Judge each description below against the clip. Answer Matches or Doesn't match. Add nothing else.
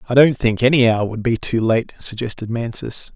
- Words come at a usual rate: Doesn't match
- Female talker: Doesn't match